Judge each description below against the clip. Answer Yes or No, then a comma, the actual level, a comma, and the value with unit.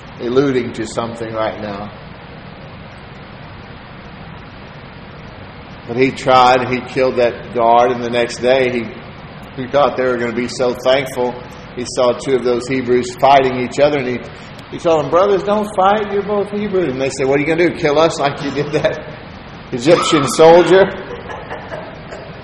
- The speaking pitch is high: No, low, 130 Hz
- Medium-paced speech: Yes, average, 170 wpm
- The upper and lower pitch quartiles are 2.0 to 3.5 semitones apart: No, average, 4.2 semitones